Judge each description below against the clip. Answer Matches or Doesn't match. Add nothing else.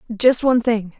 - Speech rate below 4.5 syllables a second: Doesn't match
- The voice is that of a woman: Matches